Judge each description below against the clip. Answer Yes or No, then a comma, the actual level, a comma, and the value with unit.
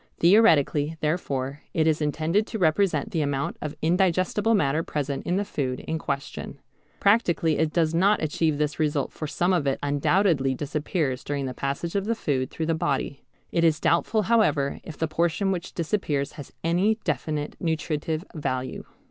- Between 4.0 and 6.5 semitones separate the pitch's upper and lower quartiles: No, average, 3.5 semitones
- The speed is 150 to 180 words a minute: Yes, average, 170 wpm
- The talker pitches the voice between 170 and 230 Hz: No, medium, 155 Hz